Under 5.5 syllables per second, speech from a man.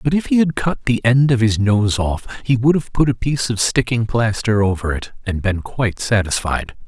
Yes: 5.1 syllables/s; male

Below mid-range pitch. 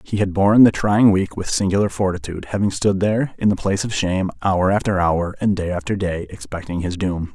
Yes: very low, 95 Hz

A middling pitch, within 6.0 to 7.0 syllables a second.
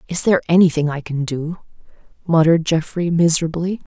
Yes: medium, 165 Hz; 6.1 syllables/s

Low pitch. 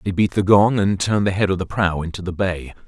Yes: very low, 95 Hz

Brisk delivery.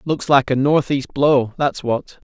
No: average, 180 wpm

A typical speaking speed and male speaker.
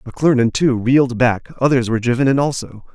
Yes: average, 185 wpm; male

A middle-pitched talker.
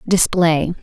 Yes: medium, 165 Hz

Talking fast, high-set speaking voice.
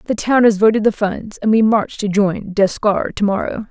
Yes: fast, 210 wpm; high, 210 Hz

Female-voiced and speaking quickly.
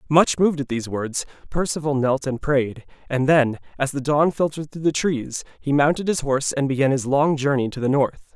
No: male; fast, 215 wpm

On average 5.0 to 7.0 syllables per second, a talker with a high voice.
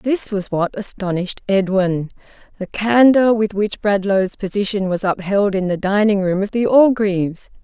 No: 4.6 syllables/s; high, 200 Hz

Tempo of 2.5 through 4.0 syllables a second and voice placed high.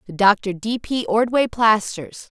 Yes: 3.7 syllables/s; high, 225 Hz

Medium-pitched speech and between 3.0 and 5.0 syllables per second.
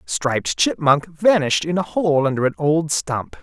Yes: medium, 150 Hz; 4.6 syllables/s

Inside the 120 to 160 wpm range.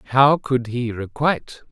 Yes: average, 140 wpm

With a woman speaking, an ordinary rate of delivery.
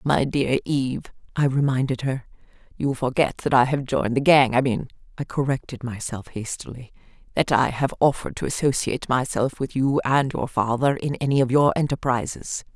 Yes: female; average, 170 wpm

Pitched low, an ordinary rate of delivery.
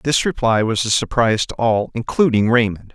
Yes: low, 115 Hz; average, 185 wpm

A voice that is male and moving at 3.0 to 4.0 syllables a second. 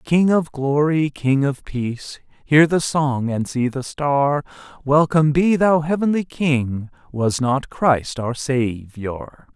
Yes: male; 3.5 syllables/s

